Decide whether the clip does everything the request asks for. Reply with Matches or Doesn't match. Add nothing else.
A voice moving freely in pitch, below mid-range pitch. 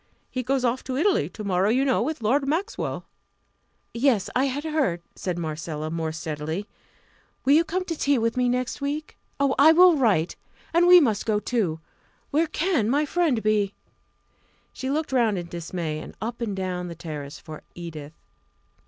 Doesn't match